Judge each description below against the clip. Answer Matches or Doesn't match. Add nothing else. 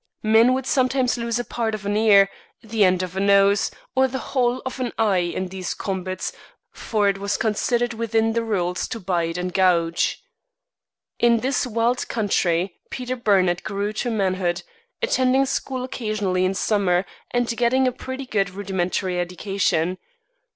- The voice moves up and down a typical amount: Matches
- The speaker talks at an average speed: Matches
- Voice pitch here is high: Matches